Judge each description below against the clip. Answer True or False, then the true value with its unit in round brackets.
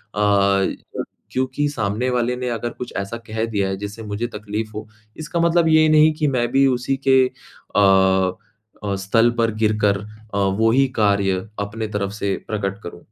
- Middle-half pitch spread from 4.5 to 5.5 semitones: False (3.8 semitones)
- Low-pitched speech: True (110 Hz)